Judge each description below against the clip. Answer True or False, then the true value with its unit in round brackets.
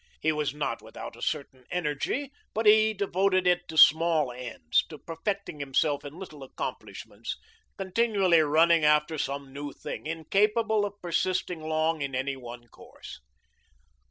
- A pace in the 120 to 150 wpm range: True (145 wpm)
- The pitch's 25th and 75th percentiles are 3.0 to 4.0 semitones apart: False (4.7 semitones)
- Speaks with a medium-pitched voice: True (160 Hz)